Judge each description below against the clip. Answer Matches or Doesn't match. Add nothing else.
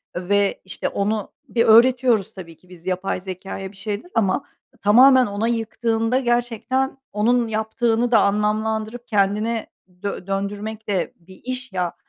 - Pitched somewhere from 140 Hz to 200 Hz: Doesn't match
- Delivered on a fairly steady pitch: Doesn't match